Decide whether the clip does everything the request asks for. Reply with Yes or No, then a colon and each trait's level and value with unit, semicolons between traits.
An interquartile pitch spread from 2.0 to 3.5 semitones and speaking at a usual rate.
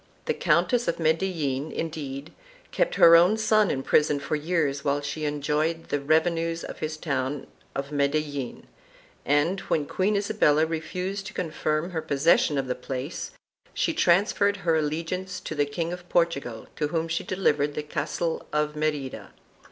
Yes: average, 3.2 semitones; average, 160 wpm